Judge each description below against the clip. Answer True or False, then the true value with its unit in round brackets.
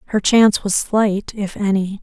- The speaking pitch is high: True (205 Hz)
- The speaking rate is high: False (180 wpm)